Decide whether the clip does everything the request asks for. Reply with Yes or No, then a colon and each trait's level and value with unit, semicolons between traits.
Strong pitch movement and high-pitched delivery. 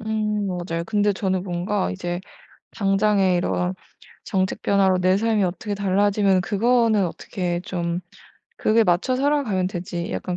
No: average, 2.8 semitones; high, 195 Hz